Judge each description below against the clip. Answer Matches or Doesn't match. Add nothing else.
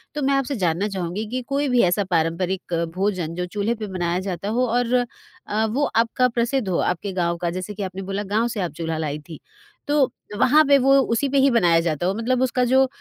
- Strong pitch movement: Matches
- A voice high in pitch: Matches